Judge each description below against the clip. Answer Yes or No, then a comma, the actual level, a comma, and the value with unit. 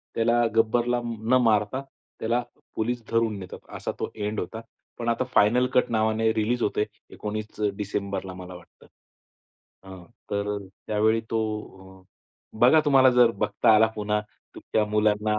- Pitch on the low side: Yes, low, 110 Hz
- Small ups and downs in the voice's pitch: Yes, narrow, 2.1 semitones